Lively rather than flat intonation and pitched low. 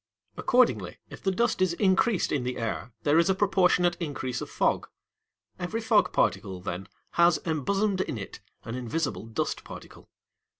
No: wide, 7.3 semitones; medium, 165 Hz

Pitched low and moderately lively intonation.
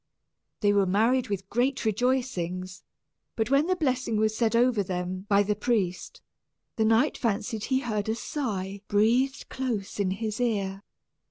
No: high, 220 Hz; average, 3.9 semitones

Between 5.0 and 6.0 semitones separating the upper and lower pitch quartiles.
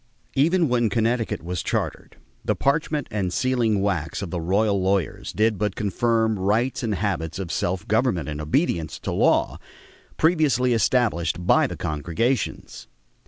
Yes: average, 5.3 semitones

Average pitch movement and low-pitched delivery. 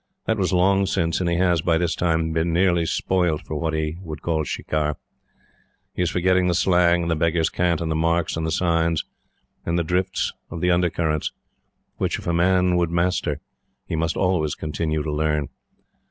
No: narrow, 1.9 semitones; very low, 85 Hz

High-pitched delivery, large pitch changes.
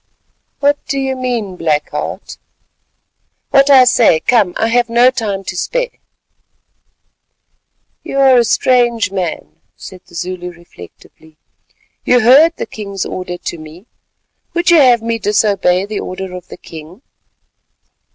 Yes: high, 215 Hz; wide, 5.8 semitones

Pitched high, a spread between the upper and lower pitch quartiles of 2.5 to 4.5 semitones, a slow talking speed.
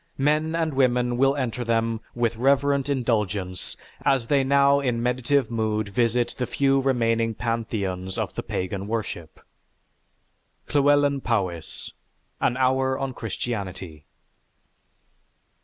No: low, 120 Hz; average, 3.8 semitones; slow, 115 wpm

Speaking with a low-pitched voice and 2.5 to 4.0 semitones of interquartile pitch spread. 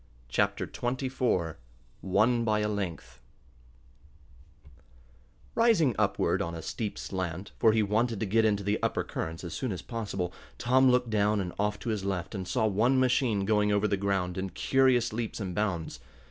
Yes: low, 105 Hz; average, 3.7 semitones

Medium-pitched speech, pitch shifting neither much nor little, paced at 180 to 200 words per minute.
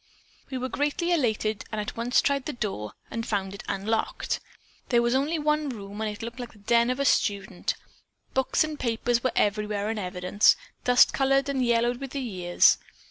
No: high, 235 Hz; average, 4.2 semitones; average, 190 wpm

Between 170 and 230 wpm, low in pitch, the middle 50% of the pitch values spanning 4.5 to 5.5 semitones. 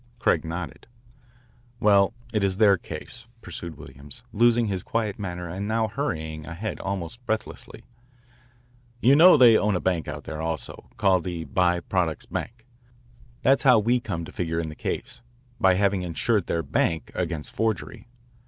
No: average, 160 wpm; very low, 95 Hz; average, 4.9 semitones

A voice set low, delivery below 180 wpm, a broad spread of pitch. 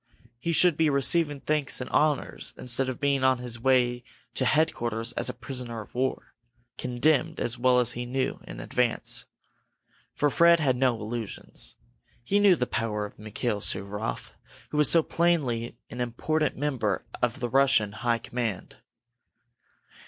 No: low, 125 Hz; average, 150 wpm; average, 3.7 semitones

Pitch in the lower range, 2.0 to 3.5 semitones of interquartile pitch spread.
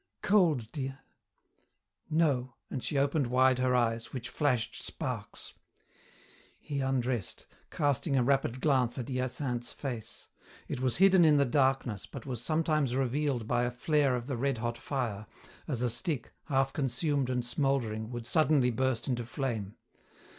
Yes: low, 130 Hz; average, 2.7 semitones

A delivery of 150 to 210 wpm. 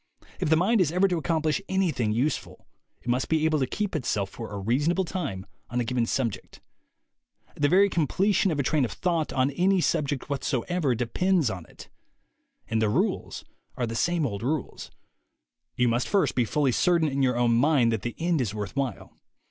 Yes: average, 195 wpm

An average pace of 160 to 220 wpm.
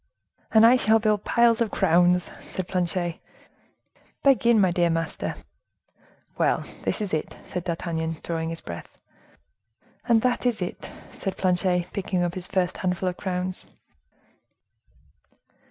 No: slow, 135 wpm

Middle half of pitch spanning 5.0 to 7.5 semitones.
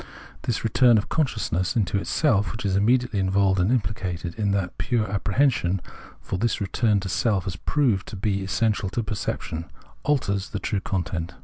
No: average, 3.2 semitones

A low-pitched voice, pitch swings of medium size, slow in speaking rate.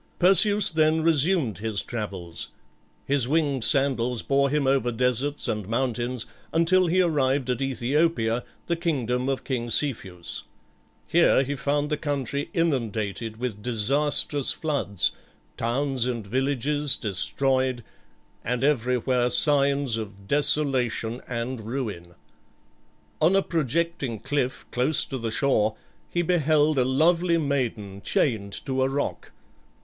Yes: low, 130 Hz; average, 4.0 semitones; slow, 125 wpm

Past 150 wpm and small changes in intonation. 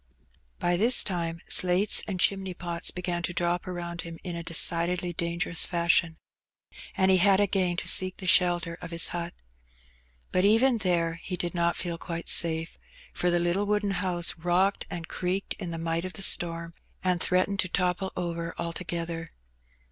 Yes: average, 170 wpm; narrow, 1.6 semitones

